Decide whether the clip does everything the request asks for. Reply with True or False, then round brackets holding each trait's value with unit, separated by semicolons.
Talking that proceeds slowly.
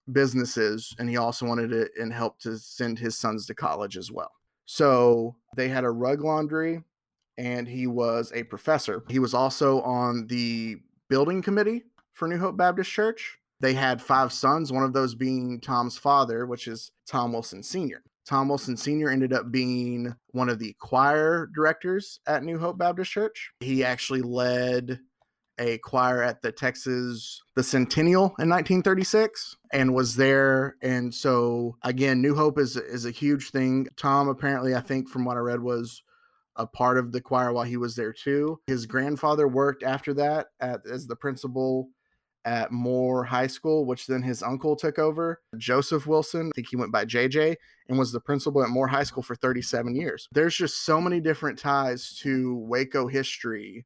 False (180 wpm)